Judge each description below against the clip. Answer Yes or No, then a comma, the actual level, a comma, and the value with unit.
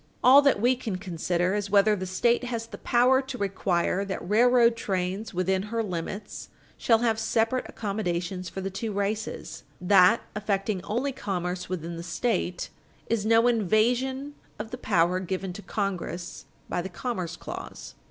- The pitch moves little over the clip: No, average, 4.0 semitones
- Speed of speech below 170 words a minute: Yes, average, 160 wpm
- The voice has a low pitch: No, high, 205 Hz